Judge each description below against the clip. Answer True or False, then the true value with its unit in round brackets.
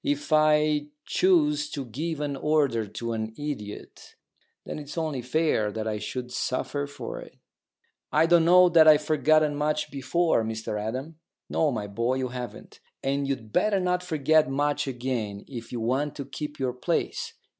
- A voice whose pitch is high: False (145 Hz)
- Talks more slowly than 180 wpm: True (165 wpm)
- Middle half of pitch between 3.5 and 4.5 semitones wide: True (4.2 semitones)